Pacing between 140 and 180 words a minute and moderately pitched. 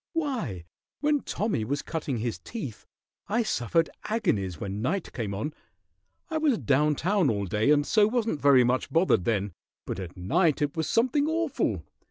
Yes: average, 170 wpm; medium, 150 Hz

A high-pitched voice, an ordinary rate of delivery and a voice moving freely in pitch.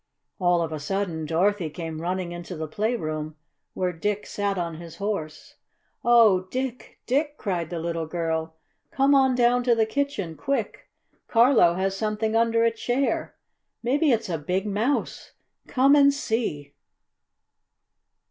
Yes: high, 200 Hz; average, 145 wpm; wide, 6.2 semitones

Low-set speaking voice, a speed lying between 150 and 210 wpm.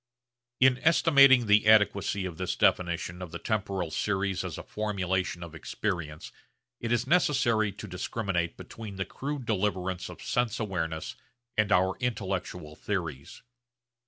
No: low, 100 Hz; slow, 135 wpm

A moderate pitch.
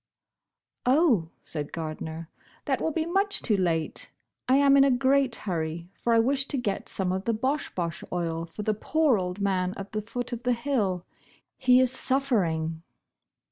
No: high, 215 Hz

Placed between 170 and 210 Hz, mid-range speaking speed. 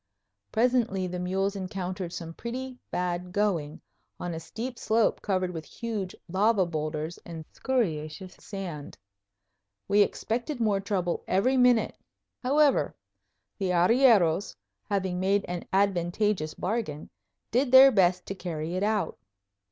No: high, 190 Hz; slow, 125 wpm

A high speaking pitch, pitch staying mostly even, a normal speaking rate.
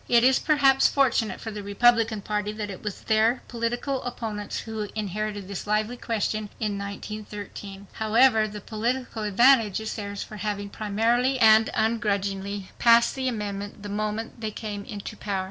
Yes: high, 215 Hz; narrow, 2.2 semitones; average, 160 wpm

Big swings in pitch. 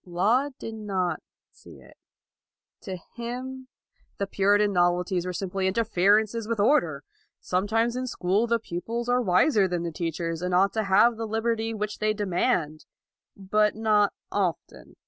No: average, 3.9 semitones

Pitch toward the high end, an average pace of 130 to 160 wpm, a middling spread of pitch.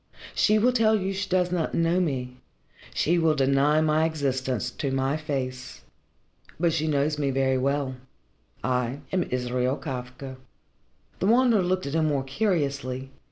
No: medium, 145 Hz; average, 155 wpm; average, 4.8 semitones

